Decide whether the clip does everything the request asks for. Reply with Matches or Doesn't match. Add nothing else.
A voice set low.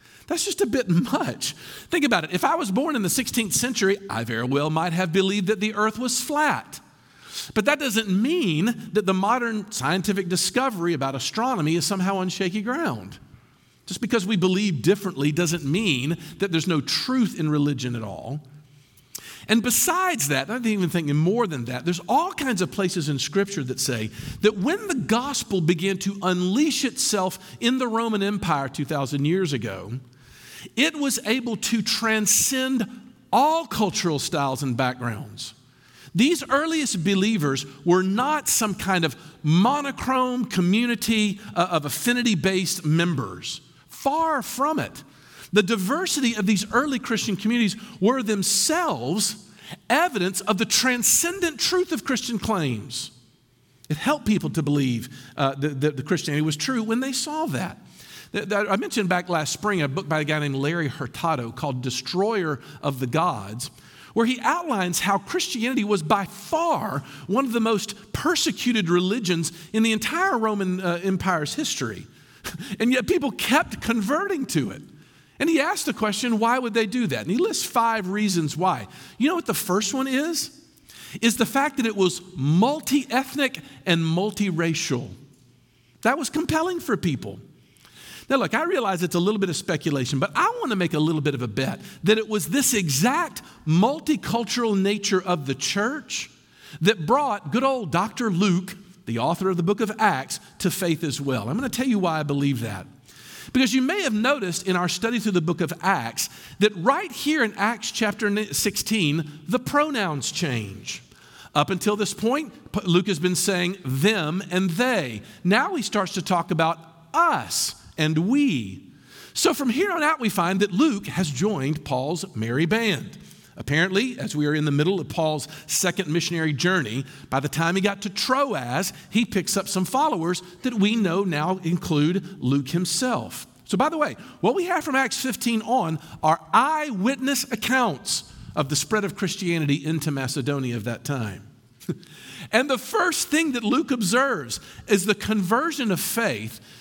Doesn't match